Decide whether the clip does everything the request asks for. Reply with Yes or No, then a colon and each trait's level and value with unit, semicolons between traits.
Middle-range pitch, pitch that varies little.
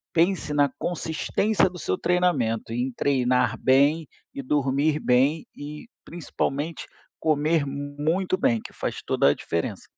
No: medium, 145 Hz; average, 3.7 semitones